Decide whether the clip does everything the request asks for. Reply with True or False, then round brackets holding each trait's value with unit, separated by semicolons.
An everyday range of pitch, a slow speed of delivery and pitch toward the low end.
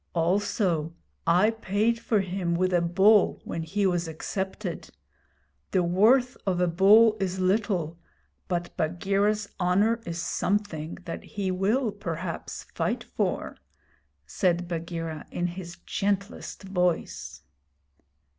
False (3.1 semitones; 115 wpm; 185 Hz)